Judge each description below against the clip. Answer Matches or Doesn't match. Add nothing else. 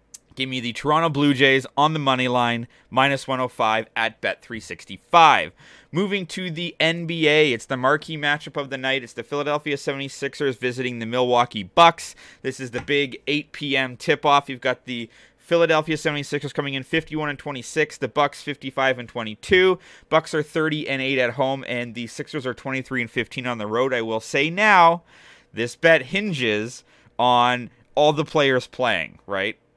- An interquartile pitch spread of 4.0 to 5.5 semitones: Doesn't match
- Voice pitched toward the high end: Doesn't match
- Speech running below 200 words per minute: Matches